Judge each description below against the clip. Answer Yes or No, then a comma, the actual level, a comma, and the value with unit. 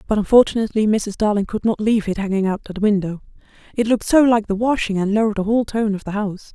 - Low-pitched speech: No, high, 210 Hz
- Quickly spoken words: Yes, fast, 250 wpm